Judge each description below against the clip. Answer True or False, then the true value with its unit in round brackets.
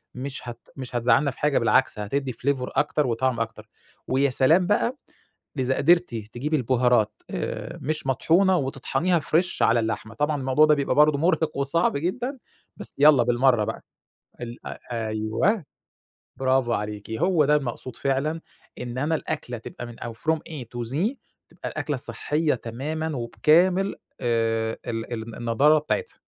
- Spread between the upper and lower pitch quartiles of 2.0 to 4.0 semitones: False (4.6 semitones)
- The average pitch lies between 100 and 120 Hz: False (135 Hz)